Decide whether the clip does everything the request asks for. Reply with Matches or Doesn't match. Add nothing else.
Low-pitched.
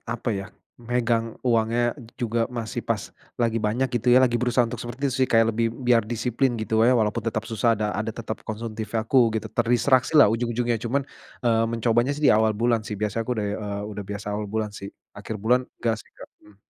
Matches